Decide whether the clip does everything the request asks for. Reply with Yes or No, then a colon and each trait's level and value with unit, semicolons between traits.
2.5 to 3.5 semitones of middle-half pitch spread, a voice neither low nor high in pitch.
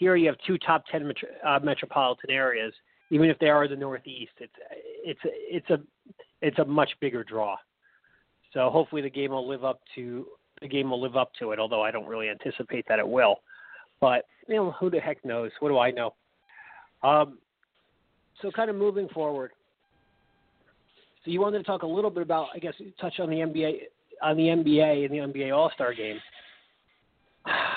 No: wide, 5.6 semitones; medium, 150 Hz